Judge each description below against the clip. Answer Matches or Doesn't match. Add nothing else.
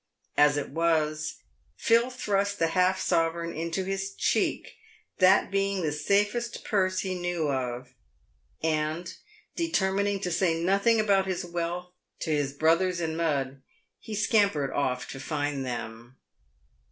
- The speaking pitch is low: Doesn't match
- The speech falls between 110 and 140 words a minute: Matches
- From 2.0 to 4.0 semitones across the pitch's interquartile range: Doesn't match